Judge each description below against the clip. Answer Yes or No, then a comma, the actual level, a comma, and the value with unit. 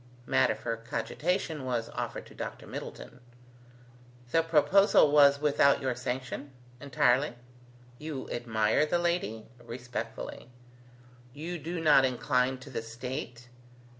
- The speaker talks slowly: Yes, slow, 115 wpm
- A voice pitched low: Yes, low, 130 Hz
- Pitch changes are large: No, average, 3.8 semitones